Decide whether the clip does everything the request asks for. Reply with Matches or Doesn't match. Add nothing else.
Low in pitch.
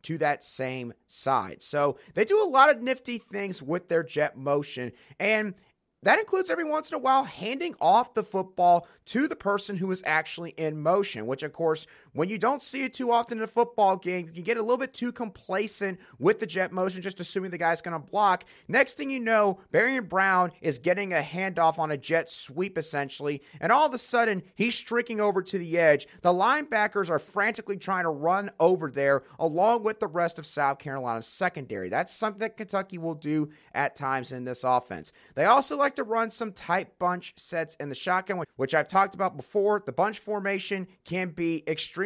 Doesn't match